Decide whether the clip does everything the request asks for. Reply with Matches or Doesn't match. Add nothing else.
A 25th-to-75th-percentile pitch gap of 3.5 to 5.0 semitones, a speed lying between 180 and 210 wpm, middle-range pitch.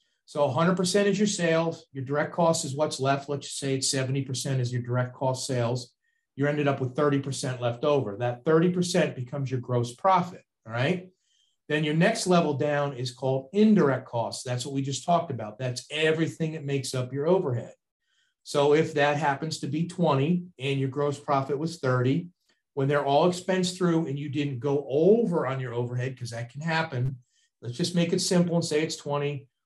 Matches